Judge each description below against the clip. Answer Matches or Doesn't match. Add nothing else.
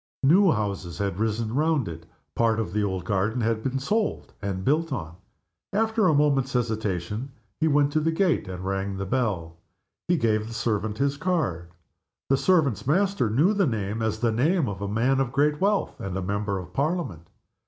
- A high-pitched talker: Doesn't match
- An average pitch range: Doesn't match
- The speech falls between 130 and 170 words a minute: Doesn't match